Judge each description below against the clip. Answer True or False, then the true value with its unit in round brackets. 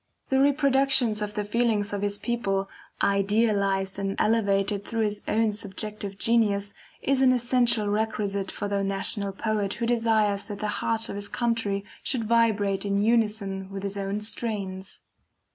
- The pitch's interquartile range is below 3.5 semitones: True (2.5 semitones)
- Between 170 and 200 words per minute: False (155 wpm)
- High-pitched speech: True (210 Hz)